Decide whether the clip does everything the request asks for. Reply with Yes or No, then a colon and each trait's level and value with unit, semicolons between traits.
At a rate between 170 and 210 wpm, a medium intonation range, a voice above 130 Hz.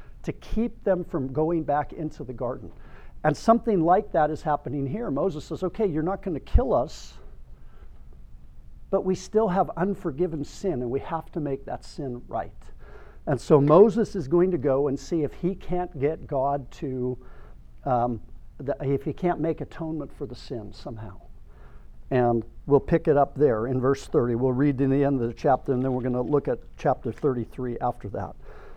No: average, 195 wpm; wide, 5.9 semitones; medium, 140 Hz